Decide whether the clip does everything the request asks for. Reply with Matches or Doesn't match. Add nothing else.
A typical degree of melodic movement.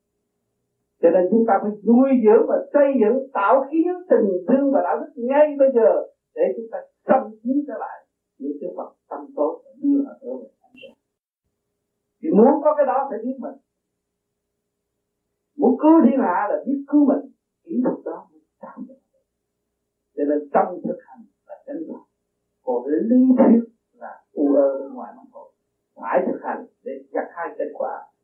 Matches